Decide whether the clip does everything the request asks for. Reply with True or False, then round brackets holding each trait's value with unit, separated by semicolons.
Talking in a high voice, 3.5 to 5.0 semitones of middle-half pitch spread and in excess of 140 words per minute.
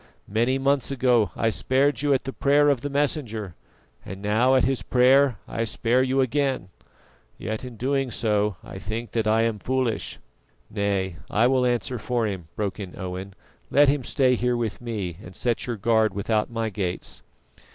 False (115 Hz; 3.8 semitones; 180 wpm)